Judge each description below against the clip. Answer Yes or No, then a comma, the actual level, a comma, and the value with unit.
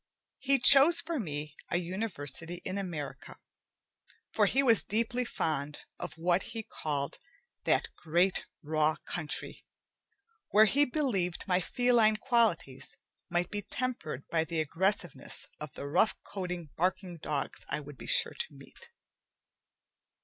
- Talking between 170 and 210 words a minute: No, slow, 135 wpm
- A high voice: No, medium, 180 Hz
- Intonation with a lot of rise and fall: Yes, wide, 6.5 semitones